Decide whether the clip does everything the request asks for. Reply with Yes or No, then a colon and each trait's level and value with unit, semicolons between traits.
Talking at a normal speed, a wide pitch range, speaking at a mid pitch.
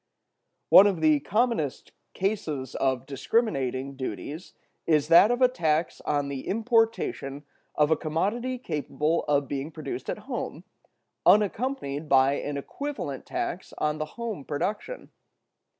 No: slow, 130 wpm; wide, 7.3 semitones; medium, 155 Hz